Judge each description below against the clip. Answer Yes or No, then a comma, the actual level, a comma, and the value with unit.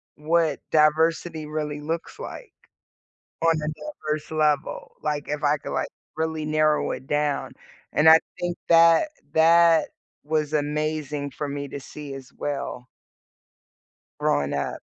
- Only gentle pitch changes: Yes, narrow, 1.5 semitones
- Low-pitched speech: No, medium, 155 Hz